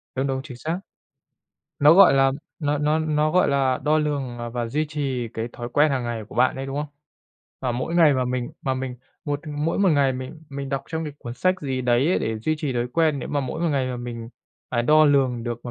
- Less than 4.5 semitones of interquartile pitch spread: Yes, average, 3.4 semitones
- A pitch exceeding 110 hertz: Yes, low, 135 Hz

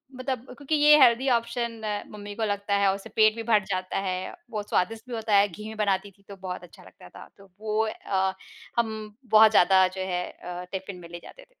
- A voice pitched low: No, high, 205 Hz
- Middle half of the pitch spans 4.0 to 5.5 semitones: No, average, 2.8 semitones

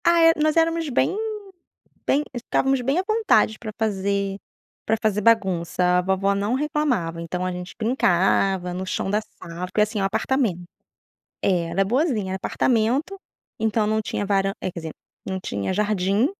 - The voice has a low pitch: No, high, 205 Hz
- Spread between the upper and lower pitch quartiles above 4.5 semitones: Yes, average, 5.1 semitones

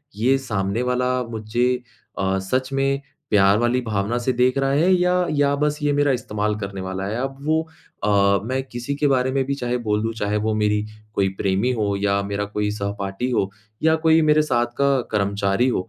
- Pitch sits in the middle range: No, low, 120 Hz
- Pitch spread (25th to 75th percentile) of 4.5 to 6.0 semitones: Yes, average, 5.0 semitones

